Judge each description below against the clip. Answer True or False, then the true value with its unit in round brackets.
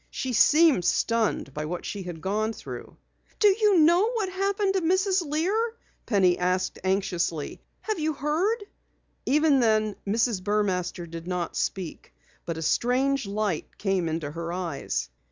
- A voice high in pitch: True (215 Hz)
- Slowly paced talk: False (150 wpm)